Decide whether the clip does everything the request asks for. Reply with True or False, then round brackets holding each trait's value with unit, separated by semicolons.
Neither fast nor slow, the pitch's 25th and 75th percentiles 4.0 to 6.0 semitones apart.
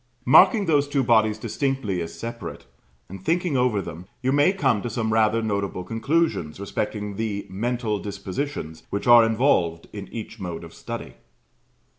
True (155 wpm; 4.8 semitones)